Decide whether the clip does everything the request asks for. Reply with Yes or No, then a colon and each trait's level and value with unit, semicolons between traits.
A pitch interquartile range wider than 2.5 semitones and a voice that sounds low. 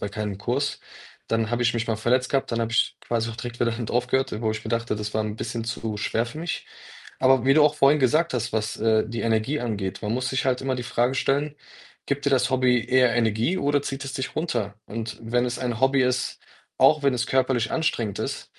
Yes: average, 2.9 semitones; low, 120 Hz